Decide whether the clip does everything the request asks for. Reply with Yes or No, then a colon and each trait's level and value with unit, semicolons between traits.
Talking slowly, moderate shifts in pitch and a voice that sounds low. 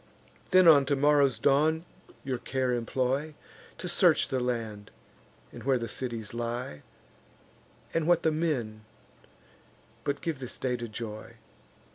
Yes: slow, 130 wpm; average, 3.9 semitones; low, 130 Hz